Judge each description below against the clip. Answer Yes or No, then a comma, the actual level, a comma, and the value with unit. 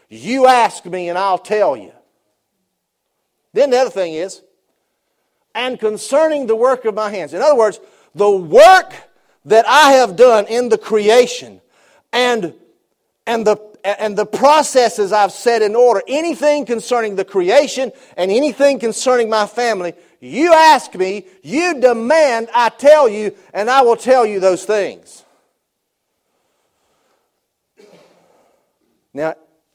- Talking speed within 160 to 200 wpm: No, slow, 135 wpm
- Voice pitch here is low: No, high, 230 Hz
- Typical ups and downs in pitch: Yes, average, 4.2 semitones